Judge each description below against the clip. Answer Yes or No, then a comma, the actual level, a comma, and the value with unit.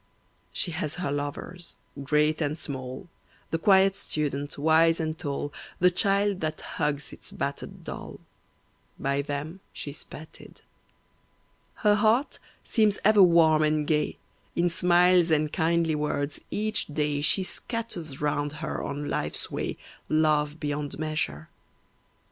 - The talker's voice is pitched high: No, medium, 155 Hz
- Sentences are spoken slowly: Yes, slow, 130 wpm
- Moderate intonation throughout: Yes, average, 3.3 semitones